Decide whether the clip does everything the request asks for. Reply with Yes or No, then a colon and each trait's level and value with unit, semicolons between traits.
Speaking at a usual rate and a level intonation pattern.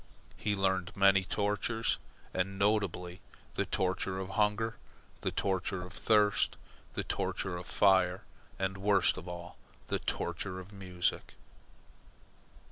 No: slow, 125 wpm; narrow, 2.1 semitones